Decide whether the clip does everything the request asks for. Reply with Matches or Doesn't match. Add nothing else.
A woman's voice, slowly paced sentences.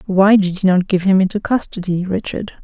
Doesn't match